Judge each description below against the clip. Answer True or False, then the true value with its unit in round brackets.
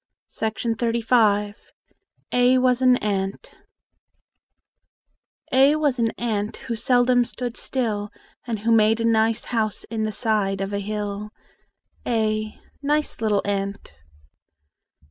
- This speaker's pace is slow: True (120 wpm)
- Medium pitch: False (225 Hz)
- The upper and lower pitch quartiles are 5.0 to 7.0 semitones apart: False (2.8 semitones)